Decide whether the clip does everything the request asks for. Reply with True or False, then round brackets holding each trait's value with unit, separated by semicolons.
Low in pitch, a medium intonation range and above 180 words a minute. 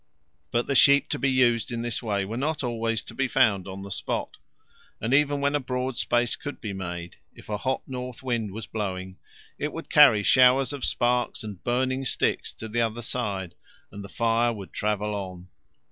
True (115 Hz; 4.0 semitones; 195 wpm)